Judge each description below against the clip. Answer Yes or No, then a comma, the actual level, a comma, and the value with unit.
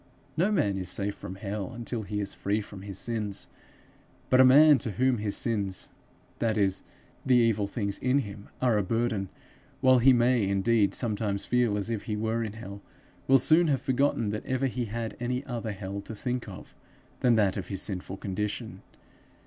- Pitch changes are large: No, average, 3.6 semitones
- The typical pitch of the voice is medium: No, low, 110 Hz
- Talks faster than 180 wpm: Yes, average, 190 wpm